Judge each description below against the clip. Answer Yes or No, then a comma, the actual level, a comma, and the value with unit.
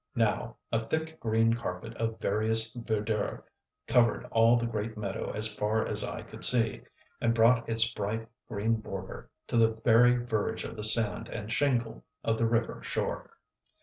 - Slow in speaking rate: No, average, 165 wpm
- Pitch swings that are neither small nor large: No, narrow, 1.3 semitones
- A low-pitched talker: Yes, low, 115 Hz